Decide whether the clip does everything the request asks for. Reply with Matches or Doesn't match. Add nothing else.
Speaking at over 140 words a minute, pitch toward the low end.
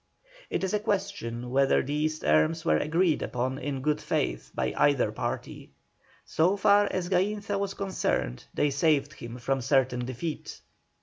Doesn't match